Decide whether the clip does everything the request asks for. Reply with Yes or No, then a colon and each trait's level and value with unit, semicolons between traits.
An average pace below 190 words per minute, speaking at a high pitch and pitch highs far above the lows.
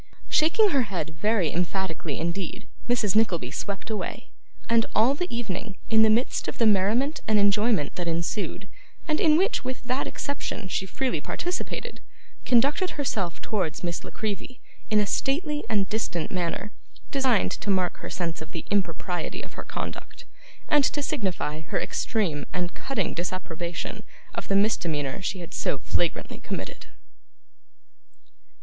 Yes: average, 150 wpm; high, 205 Hz; wide, 5.8 semitones